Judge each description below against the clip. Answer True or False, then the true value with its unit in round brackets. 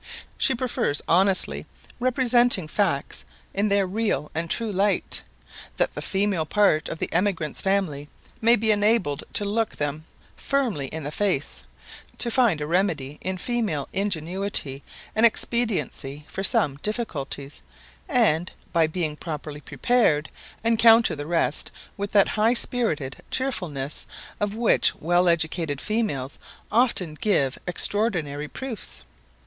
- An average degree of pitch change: False (6.5 semitones)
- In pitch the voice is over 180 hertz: True (190 Hz)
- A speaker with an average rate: False (130 wpm)